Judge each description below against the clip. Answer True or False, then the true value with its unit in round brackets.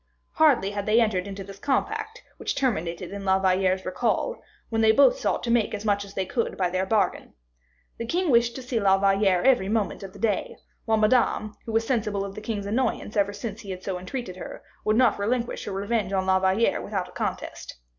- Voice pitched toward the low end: False (205 Hz)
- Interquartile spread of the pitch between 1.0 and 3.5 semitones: True (3.2 semitones)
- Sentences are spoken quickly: True (220 wpm)